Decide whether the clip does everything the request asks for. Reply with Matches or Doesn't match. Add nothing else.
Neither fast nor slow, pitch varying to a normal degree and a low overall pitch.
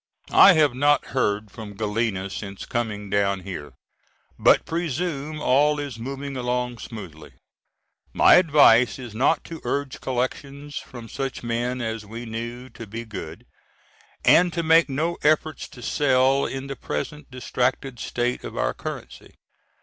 Matches